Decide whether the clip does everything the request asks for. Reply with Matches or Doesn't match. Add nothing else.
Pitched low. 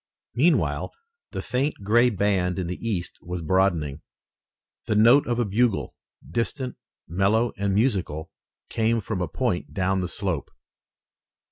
Matches